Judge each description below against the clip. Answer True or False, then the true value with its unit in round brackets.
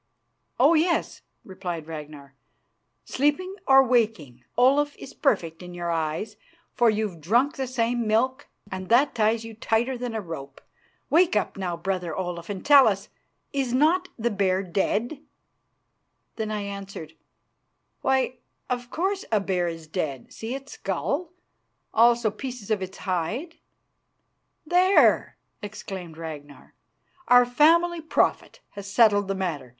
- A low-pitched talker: False (215 Hz)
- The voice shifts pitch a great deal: True (6.5 semitones)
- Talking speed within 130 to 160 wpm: True (135 wpm)